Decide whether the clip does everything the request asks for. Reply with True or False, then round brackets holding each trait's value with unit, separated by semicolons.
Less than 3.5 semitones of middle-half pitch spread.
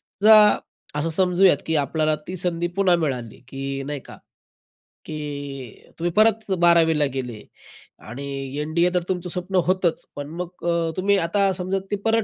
False (4.1 semitones)